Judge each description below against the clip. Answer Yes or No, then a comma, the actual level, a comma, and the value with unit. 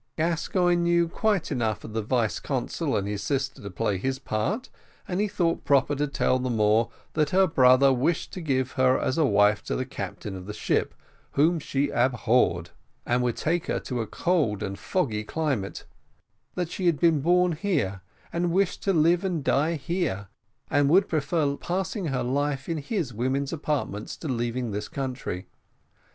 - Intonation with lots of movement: Yes, wide, 6.1 semitones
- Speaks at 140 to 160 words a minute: No, average, 180 wpm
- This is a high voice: No, medium, 140 Hz